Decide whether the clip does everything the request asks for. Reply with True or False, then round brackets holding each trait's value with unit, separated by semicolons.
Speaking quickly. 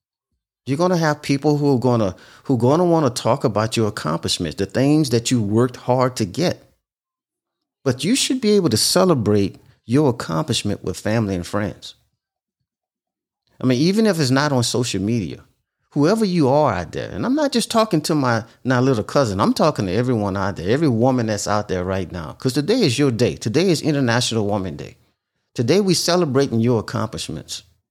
False (190 wpm)